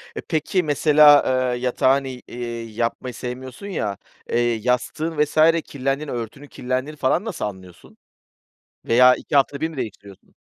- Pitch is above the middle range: No, low, 130 Hz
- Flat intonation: No, average, 3.8 semitones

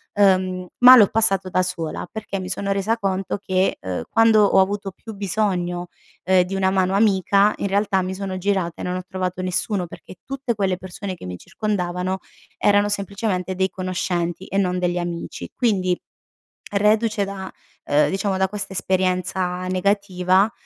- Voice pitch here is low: No, high, 190 Hz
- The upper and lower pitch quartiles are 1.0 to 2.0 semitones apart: Yes, narrow, 1.7 semitones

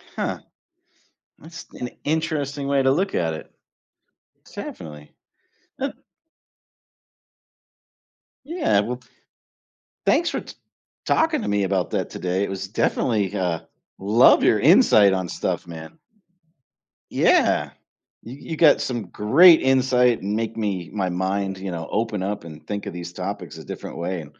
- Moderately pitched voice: No, low, 100 Hz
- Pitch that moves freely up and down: Yes, wide, 6.5 semitones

